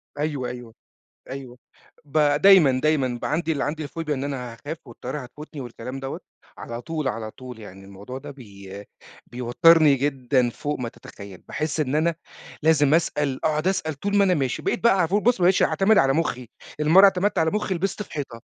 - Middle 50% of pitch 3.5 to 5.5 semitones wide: Yes, average, 4.6 semitones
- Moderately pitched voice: Yes, medium, 145 Hz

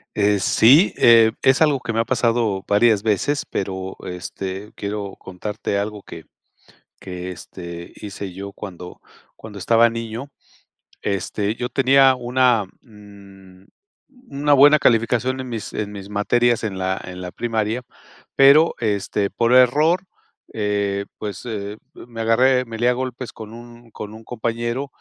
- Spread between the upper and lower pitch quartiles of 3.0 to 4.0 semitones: Yes, average, 3.5 semitones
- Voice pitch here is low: Yes, low, 110 Hz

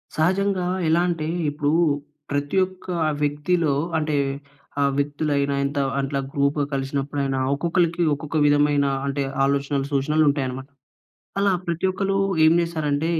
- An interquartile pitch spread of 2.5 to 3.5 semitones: Yes, average, 2.9 semitones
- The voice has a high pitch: No, medium, 145 Hz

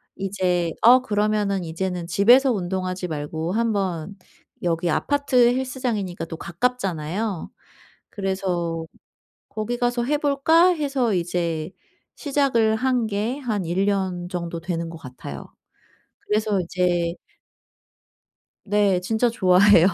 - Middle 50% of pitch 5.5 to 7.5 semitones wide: No, average, 5.1 semitones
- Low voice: No, high, 195 Hz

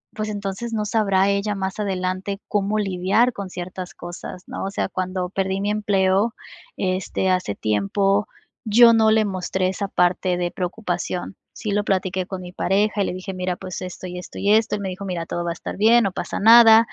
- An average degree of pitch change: No, narrow, 2.3 semitones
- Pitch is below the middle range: No, high, 195 Hz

